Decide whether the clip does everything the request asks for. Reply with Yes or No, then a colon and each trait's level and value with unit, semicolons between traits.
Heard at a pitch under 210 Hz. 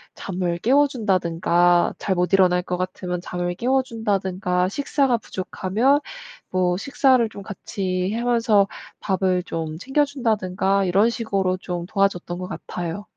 Yes: high, 190 Hz